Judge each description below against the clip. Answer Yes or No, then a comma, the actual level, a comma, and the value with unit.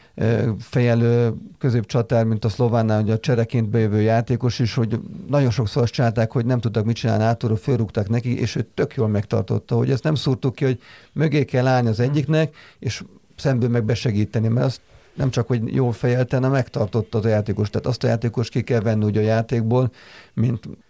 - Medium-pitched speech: No, low, 120 Hz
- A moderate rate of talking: No, fast, 190 wpm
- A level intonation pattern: Yes, narrow, 2.1 semitones